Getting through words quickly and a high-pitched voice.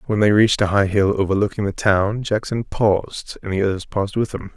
No: fast, 225 wpm; low, 100 Hz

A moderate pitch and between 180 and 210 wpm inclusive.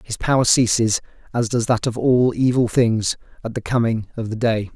No: low, 115 Hz; average, 200 wpm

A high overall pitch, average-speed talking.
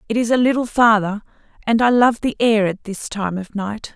No: high, 220 Hz; fast, 230 wpm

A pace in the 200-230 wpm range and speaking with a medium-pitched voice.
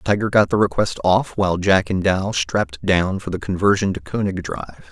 No: fast, 205 wpm; very low, 95 Hz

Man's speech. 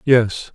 Yes: male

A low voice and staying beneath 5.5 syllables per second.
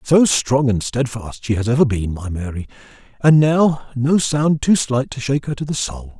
Yes: low, 130 Hz; 4.7 syllables/s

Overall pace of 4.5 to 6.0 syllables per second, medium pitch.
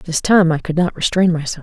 Yes: 5.5 syllables/s; medium, 165 Hz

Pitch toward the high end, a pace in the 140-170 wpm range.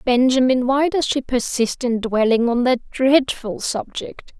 Yes: very high, 250 Hz; average, 150 wpm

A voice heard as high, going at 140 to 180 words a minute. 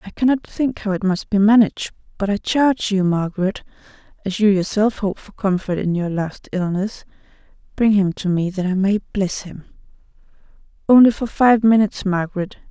Yes: high, 200 Hz; average, 175 wpm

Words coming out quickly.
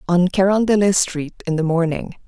No: average, 160 wpm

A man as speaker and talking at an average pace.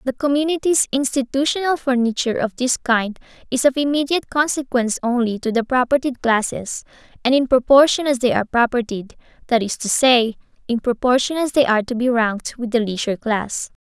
No: female; average, 170 wpm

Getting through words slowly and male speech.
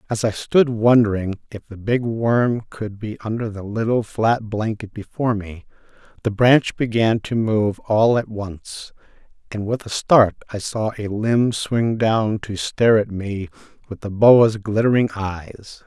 No: average, 165 wpm; male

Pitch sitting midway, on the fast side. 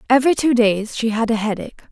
No: high, 230 Hz; fast, 220 wpm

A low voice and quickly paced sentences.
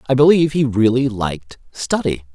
No: low, 125 Hz; average, 155 wpm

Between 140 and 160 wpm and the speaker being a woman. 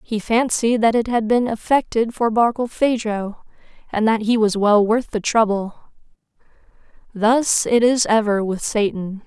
Yes: average, 150 wpm; female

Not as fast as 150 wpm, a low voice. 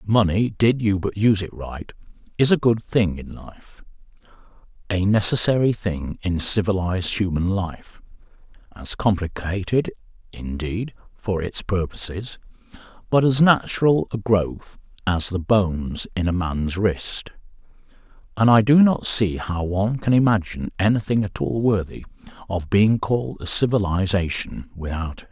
Yes: slow, 135 wpm; low, 100 Hz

